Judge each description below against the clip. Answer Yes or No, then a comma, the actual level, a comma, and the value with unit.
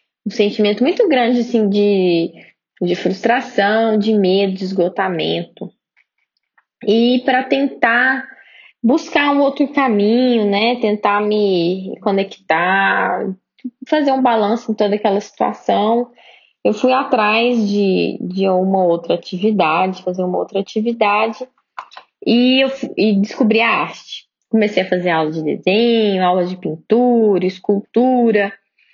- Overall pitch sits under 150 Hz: No, high, 210 Hz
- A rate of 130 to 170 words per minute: No, slow, 120 wpm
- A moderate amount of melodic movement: Yes, average, 4.0 semitones